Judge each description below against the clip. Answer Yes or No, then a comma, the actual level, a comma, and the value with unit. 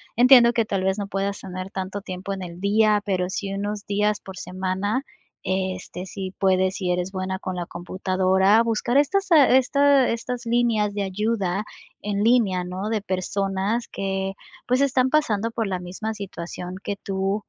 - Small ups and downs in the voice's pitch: No, average, 3.2 semitones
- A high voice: Yes, high, 200 Hz